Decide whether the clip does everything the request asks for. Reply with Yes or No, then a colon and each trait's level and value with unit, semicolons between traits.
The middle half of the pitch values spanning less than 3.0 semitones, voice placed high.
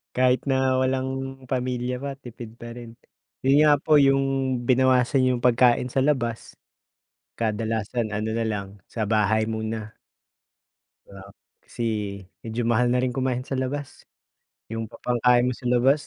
No: narrow, 2.5 semitones; low, 125 Hz